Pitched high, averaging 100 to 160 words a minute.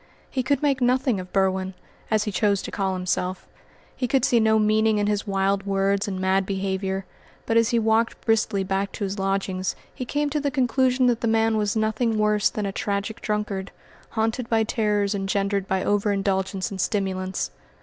No: high, 205 Hz; average, 190 wpm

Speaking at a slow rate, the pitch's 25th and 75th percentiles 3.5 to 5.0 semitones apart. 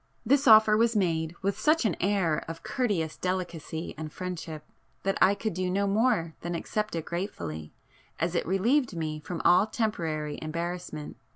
No: average, 165 wpm; average, 4.6 semitones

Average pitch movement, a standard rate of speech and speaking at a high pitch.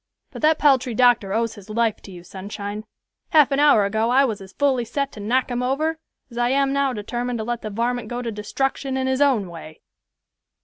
No: average, 4.2 semitones; fast, 220 wpm; high, 240 Hz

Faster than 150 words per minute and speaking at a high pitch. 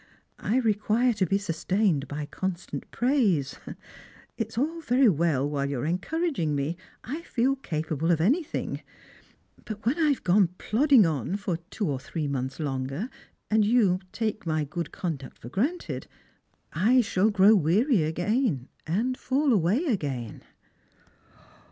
No: average, 145 wpm; high, 195 Hz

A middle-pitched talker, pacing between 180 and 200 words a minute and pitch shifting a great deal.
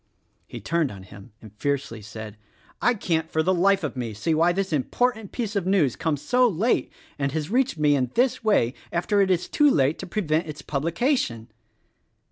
Yes: medium, 165 Hz; average, 195 wpm; wide, 6.5 semitones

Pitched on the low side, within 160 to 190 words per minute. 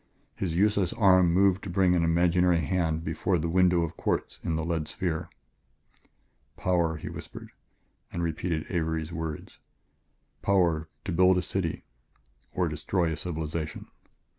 No: very low, 85 Hz; average, 140 wpm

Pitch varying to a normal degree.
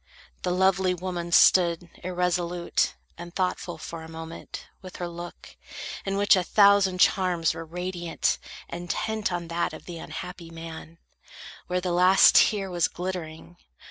No: narrow, 1.5 semitones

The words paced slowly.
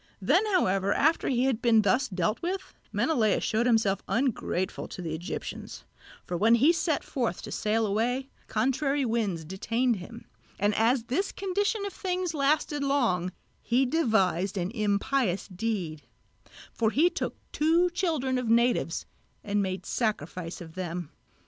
No: average, 150 wpm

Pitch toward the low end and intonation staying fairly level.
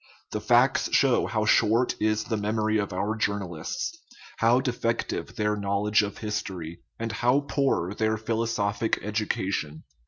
Yes: low, 110 Hz; narrow, 2.0 semitones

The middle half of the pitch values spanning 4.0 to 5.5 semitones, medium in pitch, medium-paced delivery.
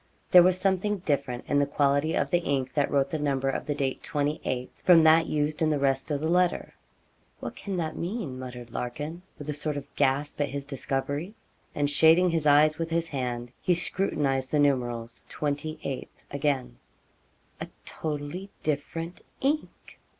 No: average, 3.1 semitones; medium, 145 Hz; average, 170 wpm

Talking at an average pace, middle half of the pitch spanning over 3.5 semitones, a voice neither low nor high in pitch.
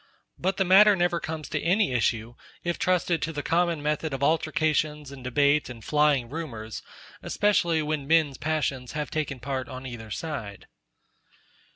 Yes: average, 160 wpm; average, 4.0 semitones; medium, 150 Hz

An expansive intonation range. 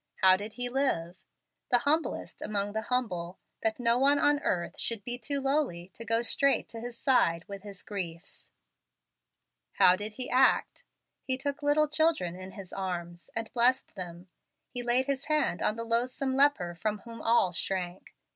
Yes: wide, 6.0 semitones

